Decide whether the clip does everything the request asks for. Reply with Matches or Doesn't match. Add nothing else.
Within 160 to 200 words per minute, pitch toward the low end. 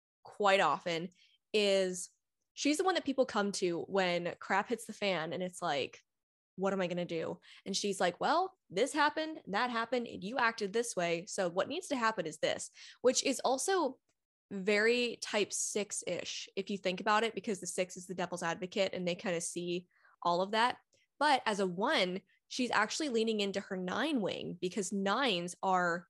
Doesn't match